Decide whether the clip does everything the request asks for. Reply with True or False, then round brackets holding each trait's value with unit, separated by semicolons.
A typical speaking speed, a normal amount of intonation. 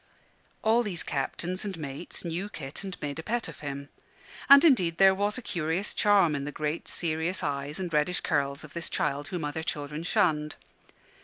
True (185 wpm; 4.5 semitones)